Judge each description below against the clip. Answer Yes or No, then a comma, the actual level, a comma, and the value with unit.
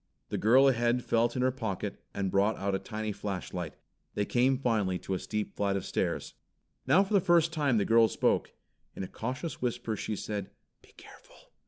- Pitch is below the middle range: Yes, low, 115 Hz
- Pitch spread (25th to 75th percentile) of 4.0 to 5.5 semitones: Yes, average, 4.3 semitones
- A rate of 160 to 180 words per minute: No, average, 195 wpm